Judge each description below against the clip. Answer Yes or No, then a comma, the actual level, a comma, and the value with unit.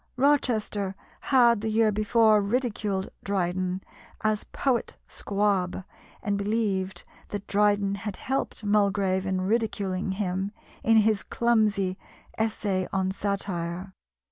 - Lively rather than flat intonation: No, narrow, 2.4 semitones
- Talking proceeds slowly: Yes, slow, 110 wpm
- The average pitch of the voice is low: No, high, 205 Hz